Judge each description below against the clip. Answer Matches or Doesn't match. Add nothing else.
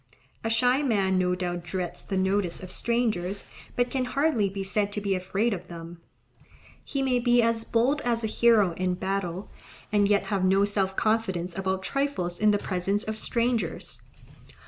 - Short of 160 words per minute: Doesn't match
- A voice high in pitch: Matches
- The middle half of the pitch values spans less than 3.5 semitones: Doesn't match